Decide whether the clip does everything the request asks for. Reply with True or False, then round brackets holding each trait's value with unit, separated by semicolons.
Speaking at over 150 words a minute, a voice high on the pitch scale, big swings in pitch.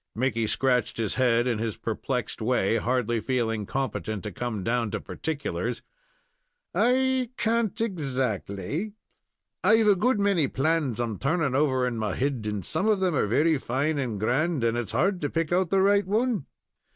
False (170 wpm; 130 Hz; 7.6 semitones)